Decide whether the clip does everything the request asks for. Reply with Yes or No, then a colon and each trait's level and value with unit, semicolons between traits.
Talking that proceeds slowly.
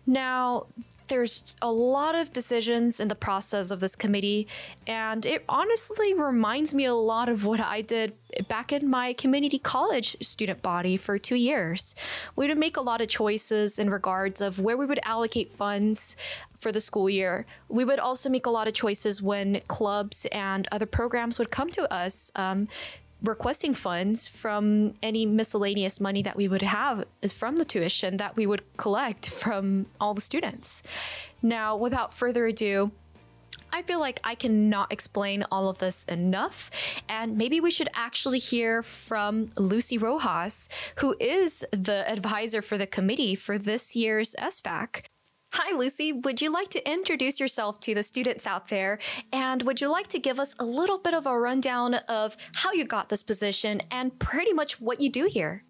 No: average, 175 wpm